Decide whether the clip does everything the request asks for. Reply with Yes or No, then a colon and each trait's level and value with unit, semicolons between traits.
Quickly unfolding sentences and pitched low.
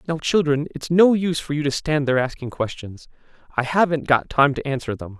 No: fast, 220 wpm; medium, 145 Hz